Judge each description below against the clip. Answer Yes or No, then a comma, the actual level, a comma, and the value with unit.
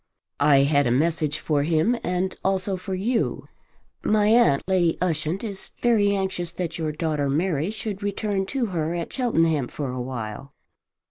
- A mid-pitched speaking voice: Yes, medium, 175 Hz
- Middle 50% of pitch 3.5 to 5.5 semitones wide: Yes, average, 4.8 semitones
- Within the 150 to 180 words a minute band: Yes, average, 160 wpm